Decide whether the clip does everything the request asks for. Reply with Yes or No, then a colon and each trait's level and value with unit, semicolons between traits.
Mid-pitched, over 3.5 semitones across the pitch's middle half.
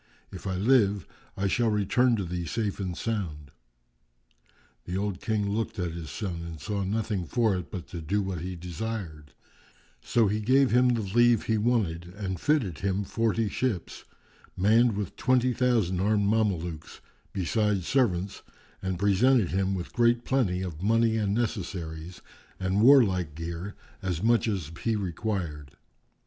No: low, 100 Hz; average, 4.1 semitones